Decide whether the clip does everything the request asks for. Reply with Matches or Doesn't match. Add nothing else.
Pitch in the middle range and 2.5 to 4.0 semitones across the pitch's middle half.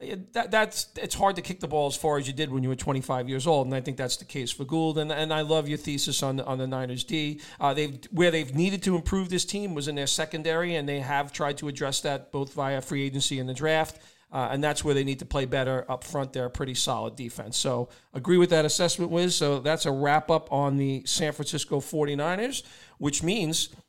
Matches